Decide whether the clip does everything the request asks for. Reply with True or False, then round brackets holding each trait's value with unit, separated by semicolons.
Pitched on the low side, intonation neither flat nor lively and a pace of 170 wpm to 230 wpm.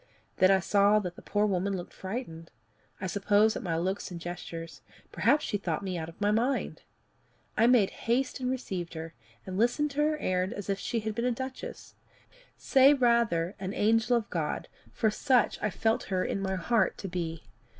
False (205 Hz; 4.6 semitones; 195 wpm)